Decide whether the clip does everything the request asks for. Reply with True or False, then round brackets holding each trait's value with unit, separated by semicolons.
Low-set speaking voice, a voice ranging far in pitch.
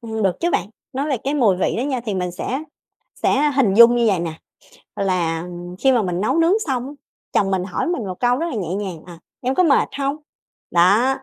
False (230 Hz; 6.3 semitones)